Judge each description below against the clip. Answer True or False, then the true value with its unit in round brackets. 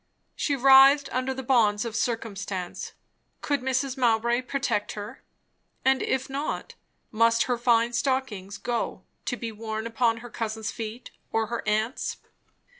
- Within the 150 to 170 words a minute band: False (140 wpm)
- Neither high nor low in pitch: False (235 Hz)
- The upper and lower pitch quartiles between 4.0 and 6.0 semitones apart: False (3.0 semitones)